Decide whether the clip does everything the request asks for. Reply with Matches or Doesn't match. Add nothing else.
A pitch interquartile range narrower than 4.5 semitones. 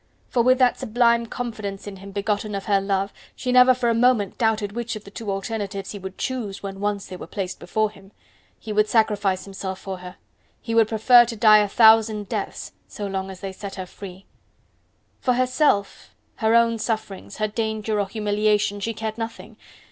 Matches